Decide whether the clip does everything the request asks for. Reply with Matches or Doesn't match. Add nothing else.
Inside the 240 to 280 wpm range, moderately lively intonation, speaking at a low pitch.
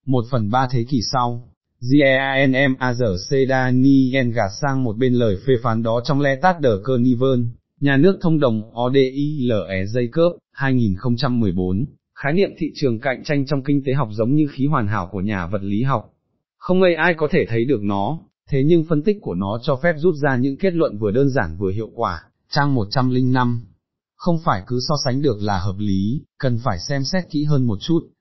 Doesn't match